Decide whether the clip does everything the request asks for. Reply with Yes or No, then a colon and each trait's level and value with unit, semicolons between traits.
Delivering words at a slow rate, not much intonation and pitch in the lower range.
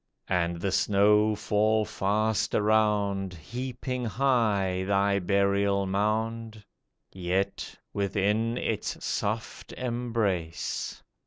Yes: slow, 85 wpm; narrow, 2.1 semitones; low, 105 Hz